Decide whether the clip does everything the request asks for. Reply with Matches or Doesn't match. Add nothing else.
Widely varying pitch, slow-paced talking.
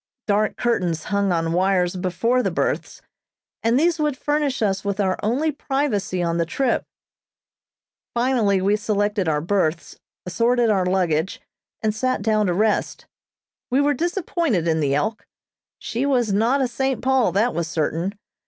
Doesn't match